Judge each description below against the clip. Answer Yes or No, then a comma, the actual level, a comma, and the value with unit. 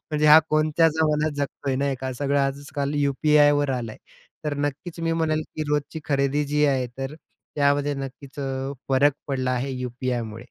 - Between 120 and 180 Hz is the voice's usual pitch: Yes, medium, 140 Hz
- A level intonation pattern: Yes, narrow, 1.9 semitones